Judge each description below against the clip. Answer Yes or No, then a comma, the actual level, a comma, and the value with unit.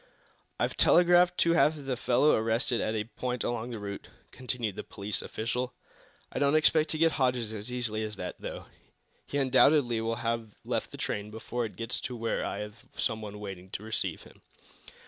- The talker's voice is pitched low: Yes, low, 115 Hz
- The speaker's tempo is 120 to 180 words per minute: No, average, 190 wpm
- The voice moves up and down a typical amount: Yes, average, 3.3 semitones